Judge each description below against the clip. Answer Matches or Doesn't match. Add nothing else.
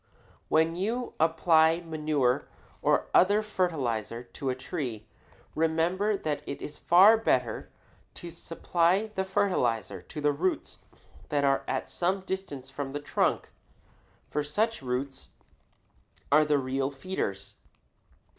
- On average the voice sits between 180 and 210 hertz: Doesn't match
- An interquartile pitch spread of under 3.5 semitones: Doesn't match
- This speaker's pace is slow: Matches